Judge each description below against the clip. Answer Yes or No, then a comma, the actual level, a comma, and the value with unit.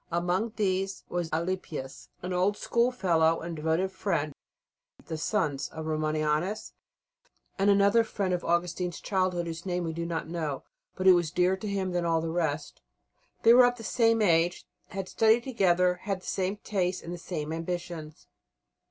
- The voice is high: No, medium, 180 Hz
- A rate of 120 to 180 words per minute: Yes, average, 170 wpm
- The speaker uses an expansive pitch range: No, average, 2.9 semitones